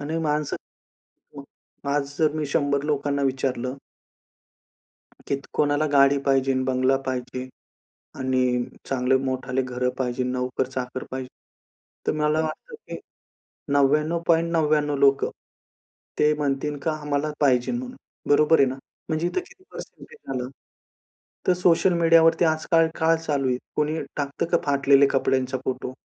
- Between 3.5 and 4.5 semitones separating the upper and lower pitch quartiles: No, average, 3.0 semitones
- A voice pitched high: No, medium, 140 Hz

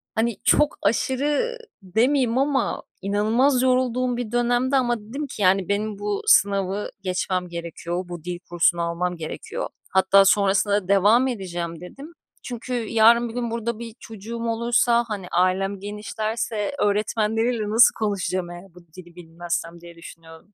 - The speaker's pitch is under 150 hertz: No, high, 210 Hz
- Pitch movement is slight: No, average, 4.5 semitones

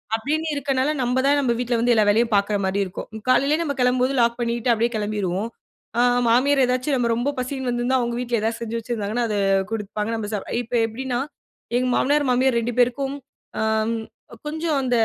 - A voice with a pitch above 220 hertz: Yes, high, 245 Hz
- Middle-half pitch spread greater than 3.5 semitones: No, average, 2.7 semitones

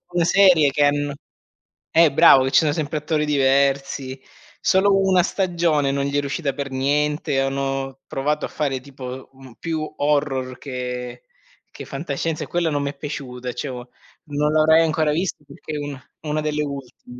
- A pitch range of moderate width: No, narrow, 2.3 semitones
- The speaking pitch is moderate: Yes, medium, 145 Hz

